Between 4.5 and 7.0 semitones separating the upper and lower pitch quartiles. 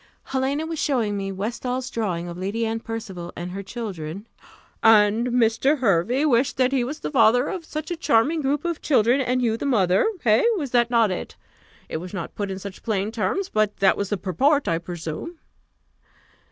Yes: wide, 5.4 semitones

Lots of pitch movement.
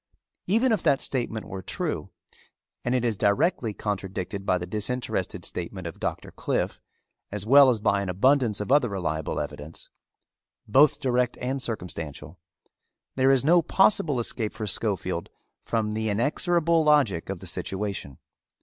Yes: wide, 5.8 semitones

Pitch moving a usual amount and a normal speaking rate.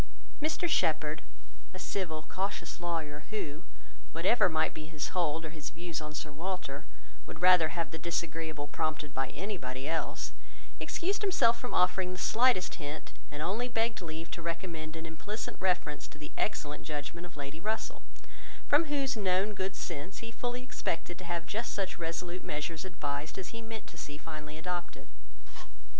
Yes: average, 3.8 semitones; average, 165 wpm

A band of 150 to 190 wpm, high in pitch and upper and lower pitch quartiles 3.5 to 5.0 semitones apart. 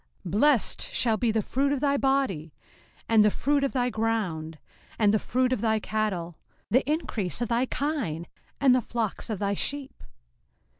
Yes: average, 180 wpm; high, 230 Hz; average, 4.6 semitones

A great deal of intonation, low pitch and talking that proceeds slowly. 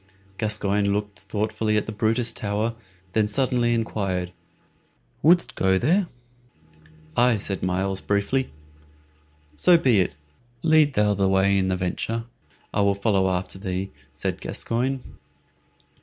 No: average, 3.3 semitones; low, 105 Hz; slow, 130 wpm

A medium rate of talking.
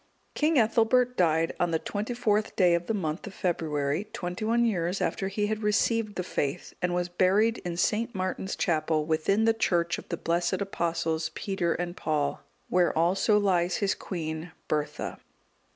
Yes: average, 170 wpm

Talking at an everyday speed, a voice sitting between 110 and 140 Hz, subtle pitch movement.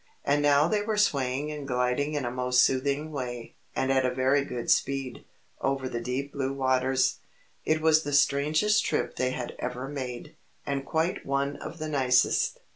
Yes: average, 180 wpm; low, 135 Hz; narrow, 2.3 semitones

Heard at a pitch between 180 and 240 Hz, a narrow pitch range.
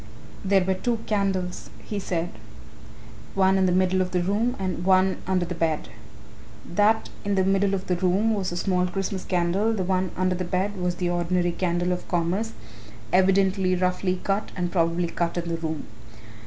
Yes: medium, 185 Hz; narrow, 1.6 semitones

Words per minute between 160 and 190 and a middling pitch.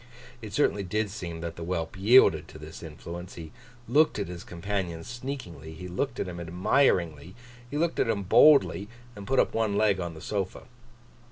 No: average, 185 wpm; very low, 95 Hz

